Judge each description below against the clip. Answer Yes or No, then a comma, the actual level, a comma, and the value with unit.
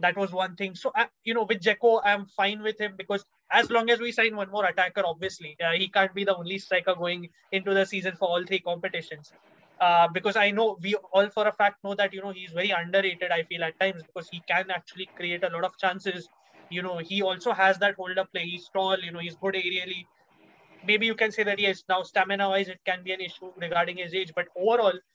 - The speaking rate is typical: No, fast, 245 wpm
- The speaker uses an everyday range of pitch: No, narrow, 2.0 semitones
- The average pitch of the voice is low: No, high, 190 Hz